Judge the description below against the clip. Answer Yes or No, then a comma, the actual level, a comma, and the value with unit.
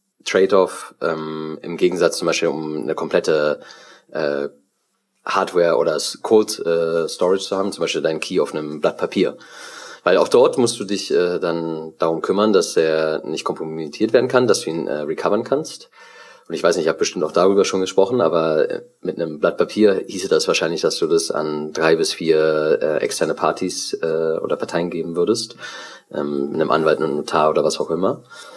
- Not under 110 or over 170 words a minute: No, fast, 190 wpm